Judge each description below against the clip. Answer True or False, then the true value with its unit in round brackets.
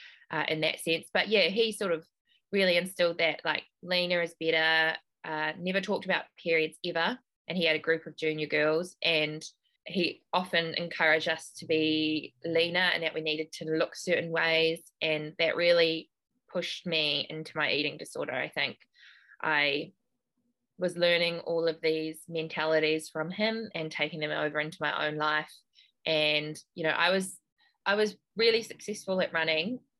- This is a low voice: False (165 Hz)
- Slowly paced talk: False (170 wpm)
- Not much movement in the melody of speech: True (2.3 semitones)